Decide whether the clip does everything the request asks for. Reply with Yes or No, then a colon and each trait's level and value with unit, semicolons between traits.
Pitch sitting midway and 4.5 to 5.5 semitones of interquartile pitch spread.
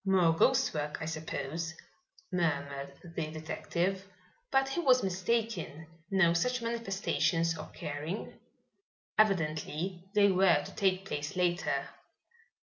No: medium, 175 Hz; average, 3.7 semitones